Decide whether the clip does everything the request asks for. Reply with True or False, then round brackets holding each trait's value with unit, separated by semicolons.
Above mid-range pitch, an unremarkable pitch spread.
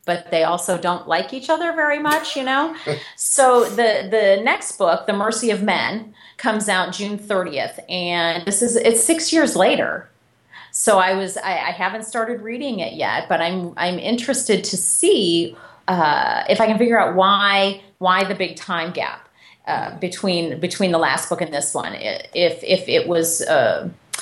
False (205 Hz; 6.8 semitones)